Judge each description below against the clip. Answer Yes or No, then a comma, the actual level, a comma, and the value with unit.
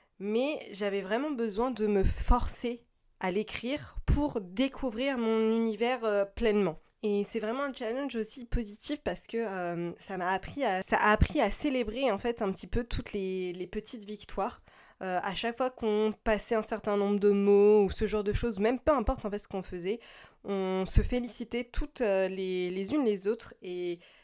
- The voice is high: Yes, high, 215 Hz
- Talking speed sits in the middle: Yes, average, 190 wpm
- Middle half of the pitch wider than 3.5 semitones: No, average, 3.2 semitones